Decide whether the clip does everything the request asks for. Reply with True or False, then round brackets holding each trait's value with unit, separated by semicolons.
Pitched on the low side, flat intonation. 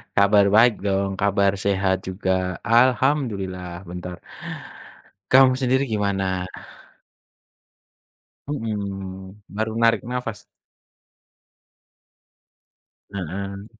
False (100 Hz; 3.2 semitones)